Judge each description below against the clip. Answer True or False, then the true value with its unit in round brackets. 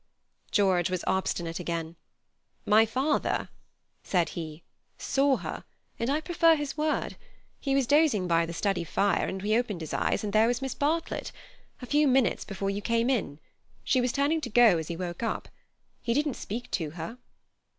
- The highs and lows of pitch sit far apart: True (7.3 semitones)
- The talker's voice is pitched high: True (225 Hz)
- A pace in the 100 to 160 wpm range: False (180 wpm)